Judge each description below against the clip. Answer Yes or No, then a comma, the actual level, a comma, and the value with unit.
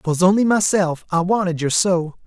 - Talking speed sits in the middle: Yes, average, 160 wpm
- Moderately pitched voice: Yes, medium, 180 Hz